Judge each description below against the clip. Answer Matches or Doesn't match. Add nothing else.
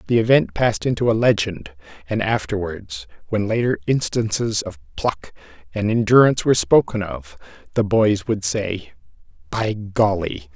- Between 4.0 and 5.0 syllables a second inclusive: Matches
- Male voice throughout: Matches